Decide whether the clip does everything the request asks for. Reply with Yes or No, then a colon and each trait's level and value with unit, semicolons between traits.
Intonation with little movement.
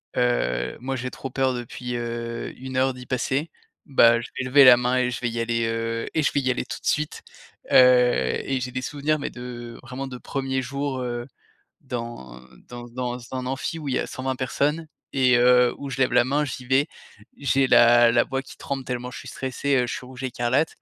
Yes: narrow, 1.9 semitones